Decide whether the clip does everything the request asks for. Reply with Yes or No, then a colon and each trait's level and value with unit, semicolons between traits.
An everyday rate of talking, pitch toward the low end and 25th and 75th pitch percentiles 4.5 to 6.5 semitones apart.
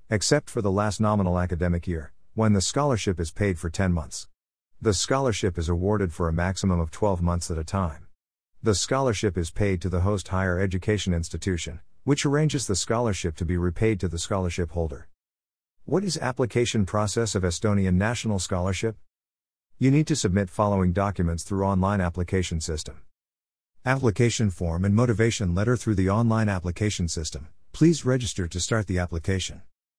No: average, 165 wpm; very low, 95 Hz; average, 3.9 semitones